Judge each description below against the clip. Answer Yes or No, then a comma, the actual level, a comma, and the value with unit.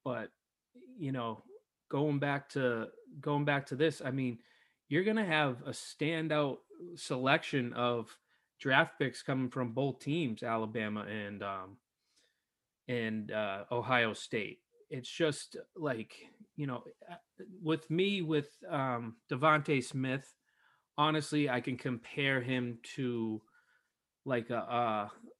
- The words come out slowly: Yes, slow, 125 wpm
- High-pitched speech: No, low, 135 Hz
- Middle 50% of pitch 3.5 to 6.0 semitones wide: Yes, average, 3.9 semitones